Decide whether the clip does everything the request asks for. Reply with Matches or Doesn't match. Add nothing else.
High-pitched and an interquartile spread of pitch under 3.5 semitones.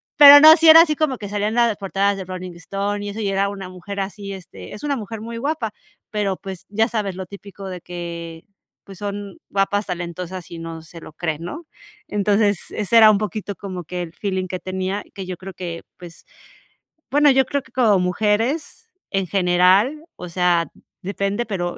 Matches